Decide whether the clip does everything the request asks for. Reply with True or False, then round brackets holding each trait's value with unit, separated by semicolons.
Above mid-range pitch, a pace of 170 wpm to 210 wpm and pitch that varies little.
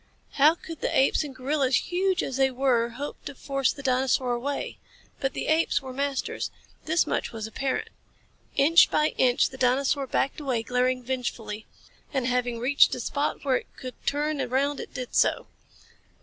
True (265 Hz; 175 wpm; 2.2 semitones)